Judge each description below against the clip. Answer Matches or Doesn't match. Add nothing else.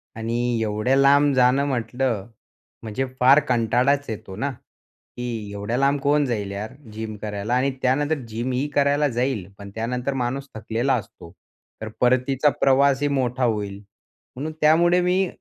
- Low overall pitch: Matches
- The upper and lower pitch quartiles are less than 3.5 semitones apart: Doesn't match